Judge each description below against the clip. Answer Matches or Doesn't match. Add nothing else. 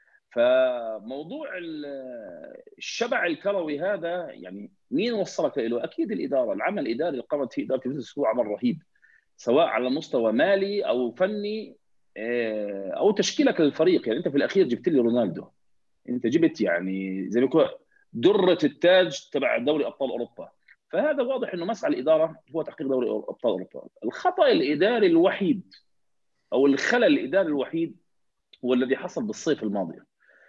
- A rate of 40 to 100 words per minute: Doesn't match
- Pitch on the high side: Matches